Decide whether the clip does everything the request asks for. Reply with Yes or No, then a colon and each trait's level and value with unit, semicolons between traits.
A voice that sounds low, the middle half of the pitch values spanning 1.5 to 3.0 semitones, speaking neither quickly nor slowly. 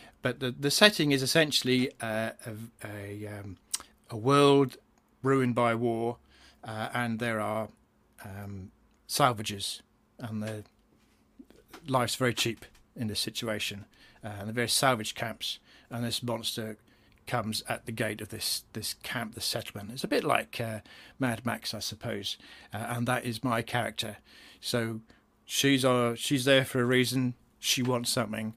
Yes: low, 115 Hz; narrow, 2.5 semitones; average, 160 wpm